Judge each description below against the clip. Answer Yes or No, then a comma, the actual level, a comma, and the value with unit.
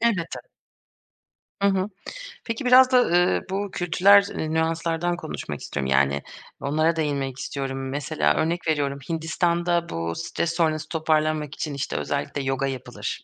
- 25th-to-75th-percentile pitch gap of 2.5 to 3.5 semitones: No, average, 4.0 semitones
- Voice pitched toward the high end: No, medium, 160 Hz